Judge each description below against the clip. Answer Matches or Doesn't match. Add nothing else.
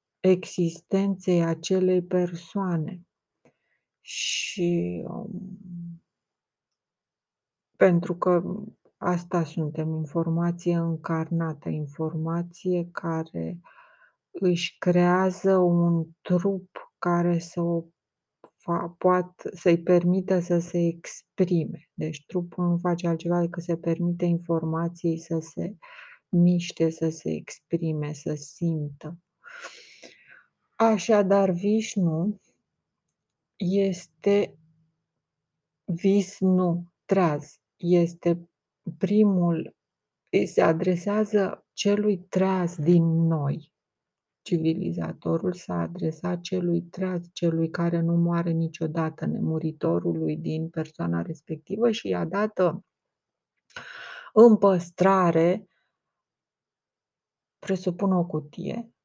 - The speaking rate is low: Matches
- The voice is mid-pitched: Matches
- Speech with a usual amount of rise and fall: Doesn't match